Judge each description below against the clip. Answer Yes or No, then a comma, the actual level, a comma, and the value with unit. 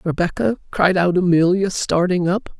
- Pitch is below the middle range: No, medium, 180 Hz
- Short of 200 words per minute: Yes, average, 140 wpm